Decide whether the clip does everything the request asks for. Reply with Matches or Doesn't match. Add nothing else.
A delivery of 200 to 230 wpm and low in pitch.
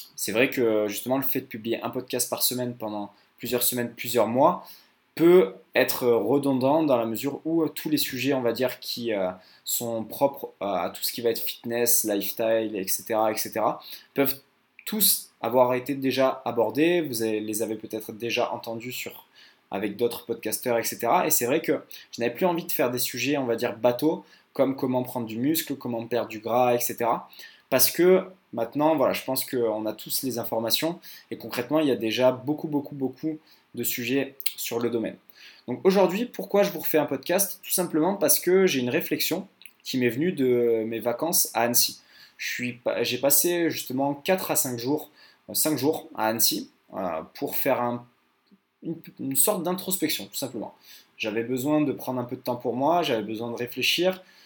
Doesn't match